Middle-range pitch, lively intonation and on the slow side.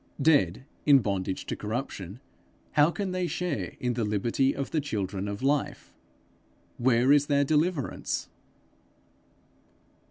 No: low, 130 Hz; wide, 6.0 semitones; slow, 125 wpm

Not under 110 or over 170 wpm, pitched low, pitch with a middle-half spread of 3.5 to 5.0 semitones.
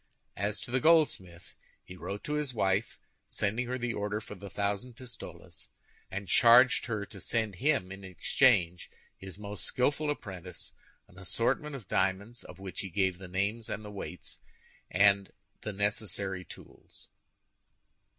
Yes: average, 150 wpm; low, 100 Hz; average, 3.8 semitones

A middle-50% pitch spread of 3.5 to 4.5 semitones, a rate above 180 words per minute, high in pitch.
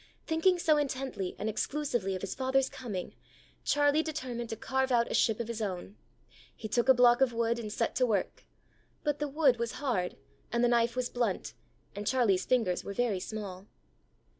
Yes: average, 3.9 semitones; average, 190 wpm; high, 240 Hz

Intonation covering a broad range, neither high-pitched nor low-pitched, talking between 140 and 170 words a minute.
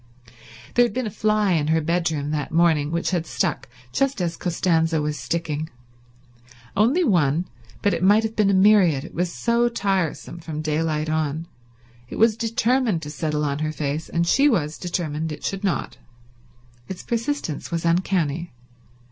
No: average, 4.9 semitones; medium, 170 Hz; average, 165 wpm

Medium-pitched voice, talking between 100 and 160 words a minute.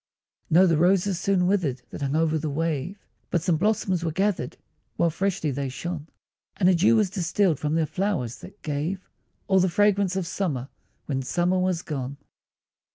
No: medium, 175 Hz; average, 175 wpm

